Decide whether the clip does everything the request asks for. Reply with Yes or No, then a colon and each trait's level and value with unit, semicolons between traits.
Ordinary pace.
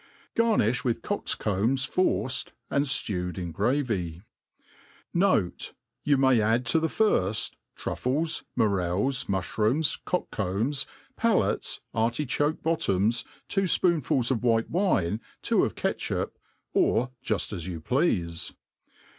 No: slow, 115 wpm